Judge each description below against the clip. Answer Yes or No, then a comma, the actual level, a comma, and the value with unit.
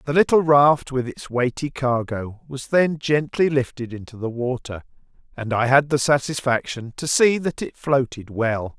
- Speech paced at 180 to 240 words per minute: No, average, 170 wpm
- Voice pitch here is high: No, low, 130 Hz